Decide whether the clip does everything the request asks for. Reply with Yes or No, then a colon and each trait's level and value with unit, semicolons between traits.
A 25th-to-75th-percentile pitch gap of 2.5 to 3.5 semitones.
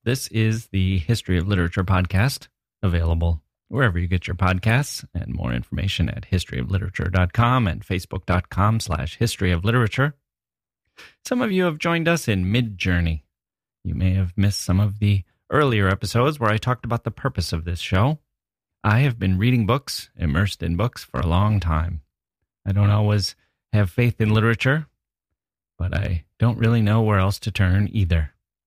No: average, 4.3 semitones